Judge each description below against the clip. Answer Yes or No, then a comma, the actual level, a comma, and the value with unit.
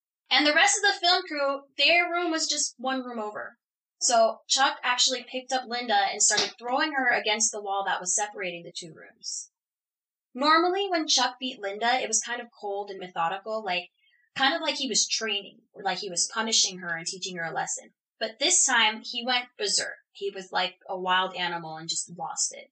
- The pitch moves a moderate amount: No, wide, 6.4 semitones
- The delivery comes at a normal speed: No, fast, 210 wpm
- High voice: Yes, high, 240 Hz